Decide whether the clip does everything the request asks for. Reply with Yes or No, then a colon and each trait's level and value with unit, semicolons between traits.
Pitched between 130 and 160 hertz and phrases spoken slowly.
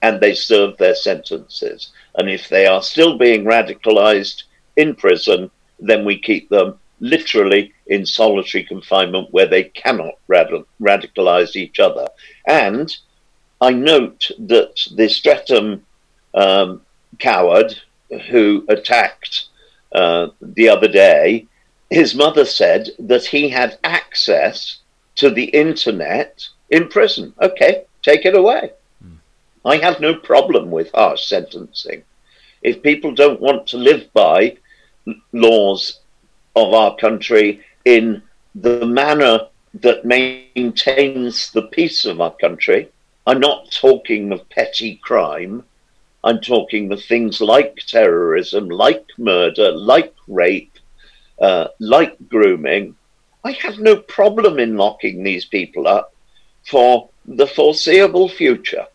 Yes: medium, 140 Hz; slow, 120 wpm